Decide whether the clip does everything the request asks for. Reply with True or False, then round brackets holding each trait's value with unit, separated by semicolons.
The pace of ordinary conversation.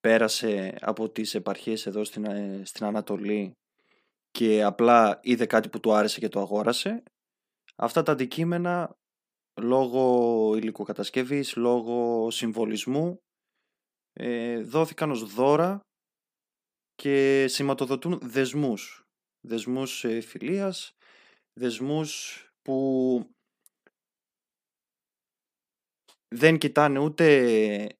False (80 wpm)